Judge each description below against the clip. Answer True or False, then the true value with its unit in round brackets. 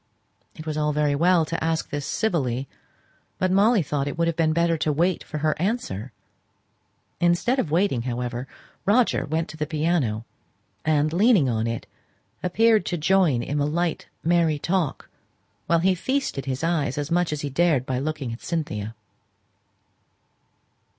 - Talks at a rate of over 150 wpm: True (165 wpm)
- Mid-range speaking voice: True (155 Hz)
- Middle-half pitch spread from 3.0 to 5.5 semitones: True (3.8 semitones)